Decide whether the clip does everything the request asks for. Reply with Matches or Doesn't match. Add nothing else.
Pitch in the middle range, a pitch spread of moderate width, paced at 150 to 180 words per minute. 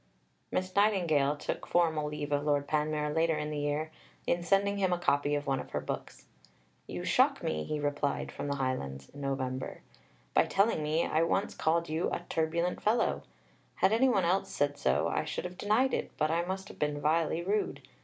Doesn't match